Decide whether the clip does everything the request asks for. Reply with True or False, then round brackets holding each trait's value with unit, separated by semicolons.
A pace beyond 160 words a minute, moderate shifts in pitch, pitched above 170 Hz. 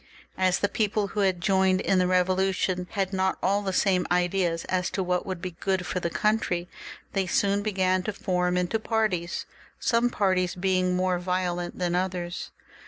False (175 wpm; 1.4 semitones; 185 Hz)